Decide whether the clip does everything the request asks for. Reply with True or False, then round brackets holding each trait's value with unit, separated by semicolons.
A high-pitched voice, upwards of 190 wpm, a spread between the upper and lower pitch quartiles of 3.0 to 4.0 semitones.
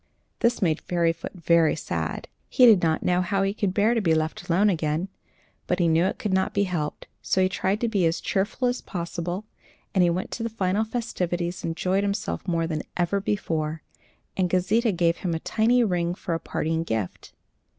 False (180 Hz; 200 wpm; 3.3 semitones)